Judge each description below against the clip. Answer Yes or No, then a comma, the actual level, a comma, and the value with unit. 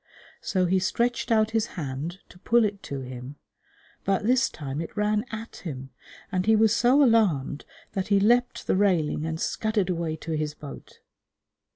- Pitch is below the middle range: No, high, 190 Hz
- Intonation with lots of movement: Yes, wide, 6.0 semitones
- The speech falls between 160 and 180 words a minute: Yes, average, 175 wpm